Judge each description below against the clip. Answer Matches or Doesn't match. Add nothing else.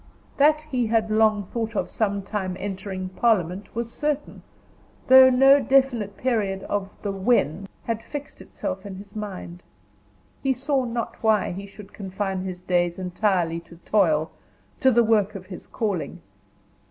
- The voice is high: Matches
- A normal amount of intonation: Matches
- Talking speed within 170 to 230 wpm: Doesn't match